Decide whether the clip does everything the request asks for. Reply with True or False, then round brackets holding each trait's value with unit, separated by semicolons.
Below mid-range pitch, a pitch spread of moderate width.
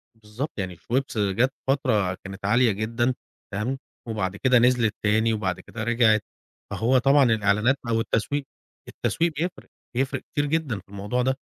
True (115 Hz; 4.0 semitones)